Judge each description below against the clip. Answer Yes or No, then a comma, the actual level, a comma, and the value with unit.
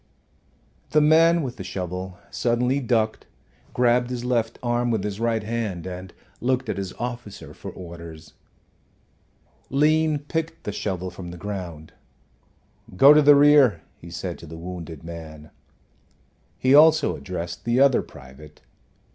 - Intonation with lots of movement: Yes, wide, 6.7 semitones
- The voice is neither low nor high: No, low, 110 Hz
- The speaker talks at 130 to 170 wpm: Yes, average, 140 wpm